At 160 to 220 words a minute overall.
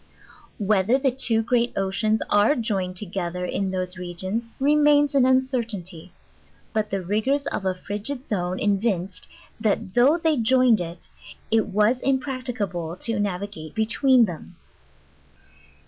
No: average, 140 wpm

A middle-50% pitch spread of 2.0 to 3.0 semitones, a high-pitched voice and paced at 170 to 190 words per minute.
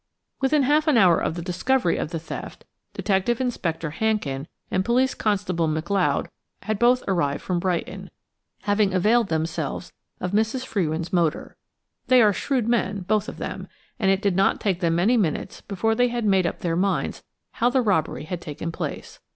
No: average, 5.2 semitones; high, 195 Hz; average, 175 wpm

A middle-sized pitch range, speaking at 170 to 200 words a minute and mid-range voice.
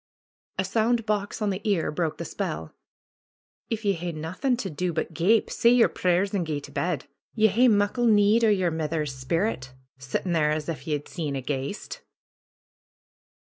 No: wide, 5.7 semitones; average, 180 wpm; medium, 180 Hz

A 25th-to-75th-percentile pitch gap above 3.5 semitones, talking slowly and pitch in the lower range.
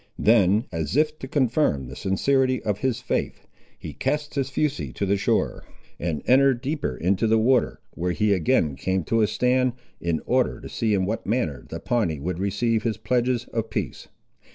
No: wide, 5.5 semitones; average, 185 wpm; low, 115 Hz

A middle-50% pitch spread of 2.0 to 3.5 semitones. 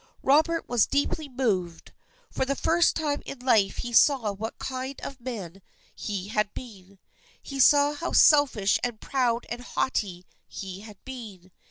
No: average, 5.3 semitones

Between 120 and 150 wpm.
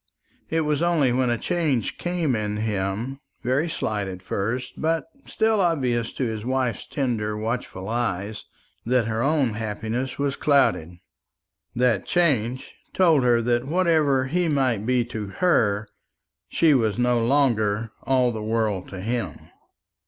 Yes: average, 145 wpm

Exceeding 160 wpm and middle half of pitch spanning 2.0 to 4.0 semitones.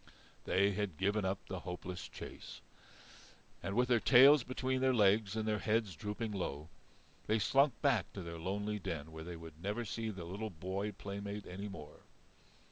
Yes: average, 175 wpm; average, 3.4 semitones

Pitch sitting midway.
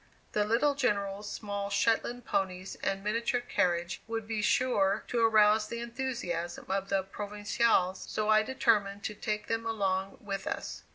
No: high, 210 Hz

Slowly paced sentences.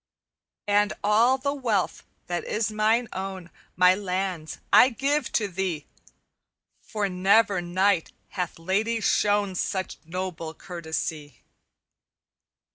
Yes: slow, 110 wpm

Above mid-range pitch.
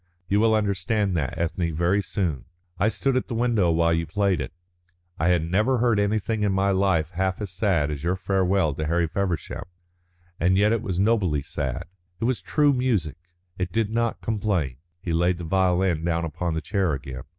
No: very low, 95 Hz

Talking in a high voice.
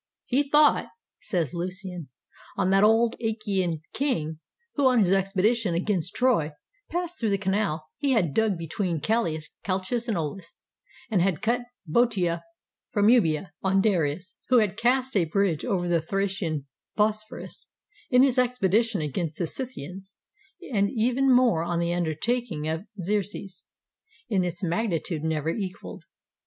Yes: high, 195 Hz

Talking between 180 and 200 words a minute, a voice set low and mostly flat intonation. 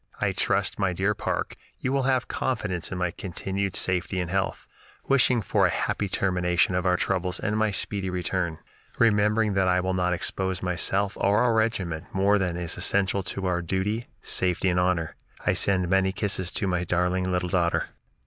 Yes: average, 185 wpm; very low, 95 Hz; narrow, 2.0 semitones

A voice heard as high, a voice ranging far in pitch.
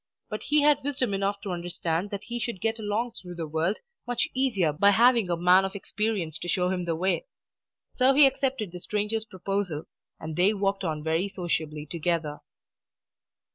No: high, 195 Hz; average, 4.6 semitones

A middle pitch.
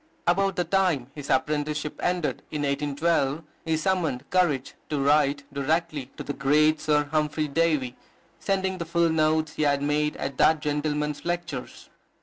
Yes: medium, 150 Hz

